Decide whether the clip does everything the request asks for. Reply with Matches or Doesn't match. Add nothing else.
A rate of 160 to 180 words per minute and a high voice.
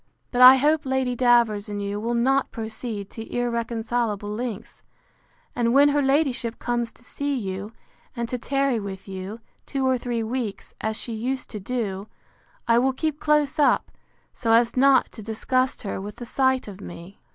Matches